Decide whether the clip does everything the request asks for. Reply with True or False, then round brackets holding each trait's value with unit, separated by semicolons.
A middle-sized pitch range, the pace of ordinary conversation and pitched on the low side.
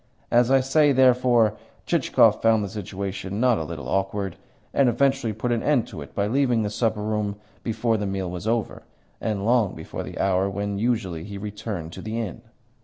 True (3.5 semitones; 190 wpm; 105 Hz)